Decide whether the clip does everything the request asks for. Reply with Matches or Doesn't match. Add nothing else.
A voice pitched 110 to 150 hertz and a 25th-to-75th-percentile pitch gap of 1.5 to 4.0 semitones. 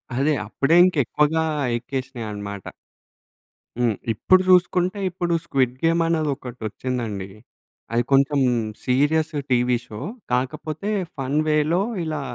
Doesn't match